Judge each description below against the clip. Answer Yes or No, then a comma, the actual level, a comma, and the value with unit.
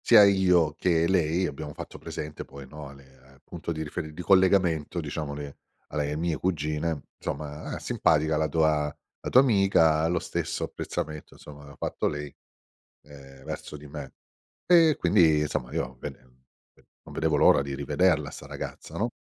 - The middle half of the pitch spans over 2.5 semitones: Yes, average, 2.9 semitones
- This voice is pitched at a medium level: No, very low, 75 Hz